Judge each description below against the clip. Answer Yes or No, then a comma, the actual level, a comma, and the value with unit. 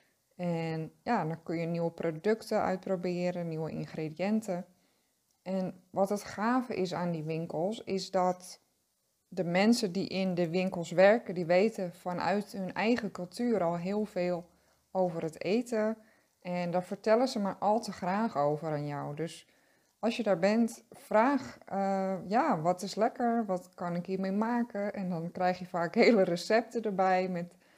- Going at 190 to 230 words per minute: No, average, 160 wpm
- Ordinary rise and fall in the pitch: Yes, average, 3.2 semitones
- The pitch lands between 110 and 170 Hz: No, medium, 185 Hz